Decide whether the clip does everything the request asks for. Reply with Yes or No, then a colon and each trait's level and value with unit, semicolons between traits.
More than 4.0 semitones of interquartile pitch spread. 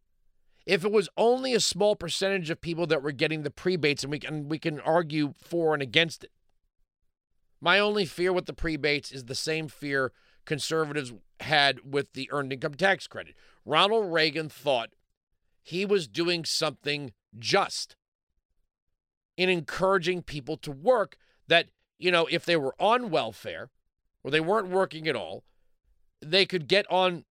Yes: average, 4.5 semitones